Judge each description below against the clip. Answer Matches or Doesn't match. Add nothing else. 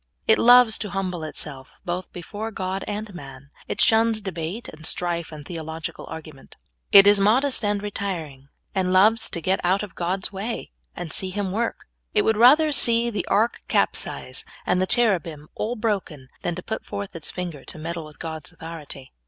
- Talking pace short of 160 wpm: Doesn't match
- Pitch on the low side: Doesn't match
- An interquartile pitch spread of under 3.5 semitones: Doesn't match